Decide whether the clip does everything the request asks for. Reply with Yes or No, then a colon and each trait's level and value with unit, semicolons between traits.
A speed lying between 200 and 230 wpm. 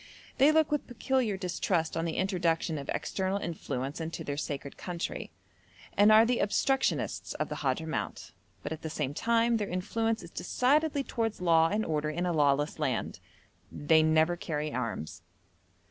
No: average, 160 wpm